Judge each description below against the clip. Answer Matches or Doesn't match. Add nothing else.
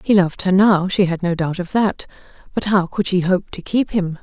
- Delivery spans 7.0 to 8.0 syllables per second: Doesn't match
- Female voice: Matches